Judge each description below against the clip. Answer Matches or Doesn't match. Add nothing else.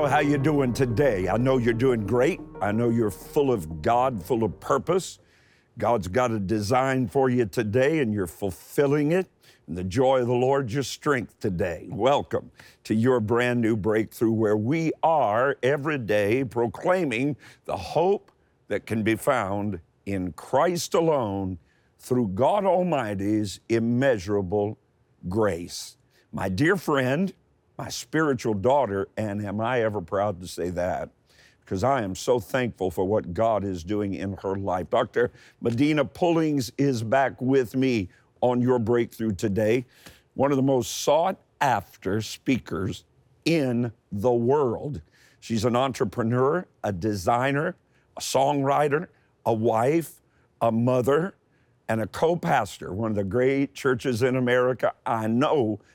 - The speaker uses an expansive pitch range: Doesn't match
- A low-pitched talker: Matches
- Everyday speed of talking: Matches